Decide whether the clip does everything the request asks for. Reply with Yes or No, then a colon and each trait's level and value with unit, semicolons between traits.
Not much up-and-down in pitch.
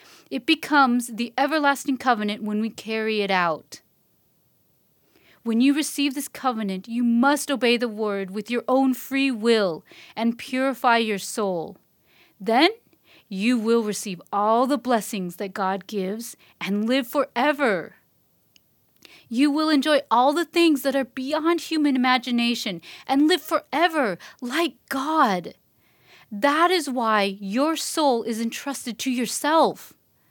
No: average, 4.7 semitones